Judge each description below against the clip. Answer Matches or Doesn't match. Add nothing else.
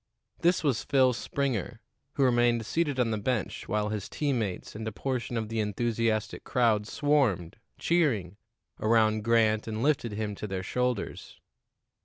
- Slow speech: Doesn't match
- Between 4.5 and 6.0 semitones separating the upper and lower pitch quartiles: Doesn't match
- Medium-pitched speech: Doesn't match